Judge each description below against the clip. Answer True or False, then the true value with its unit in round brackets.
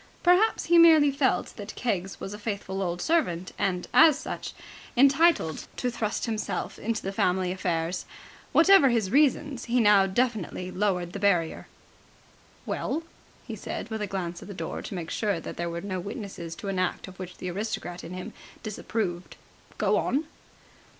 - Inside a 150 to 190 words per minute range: True (170 wpm)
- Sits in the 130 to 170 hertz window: False (200 Hz)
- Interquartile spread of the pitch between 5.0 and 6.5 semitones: True (5.3 semitones)